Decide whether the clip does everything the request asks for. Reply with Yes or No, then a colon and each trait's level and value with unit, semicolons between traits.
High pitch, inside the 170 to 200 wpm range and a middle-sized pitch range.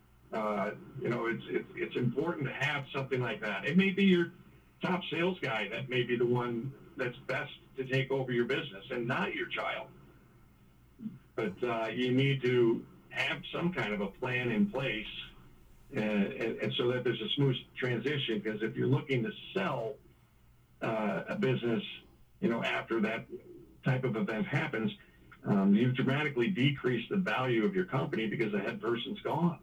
No: low, 130 Hz; average, 175 wpm; average, 3.6 semitones